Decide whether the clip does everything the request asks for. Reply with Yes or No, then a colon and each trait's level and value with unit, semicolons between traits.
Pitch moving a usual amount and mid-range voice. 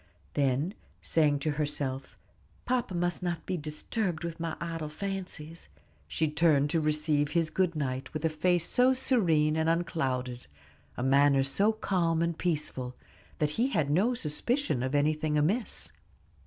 Yes: average, 3.3 semitones; medium, 160 Hz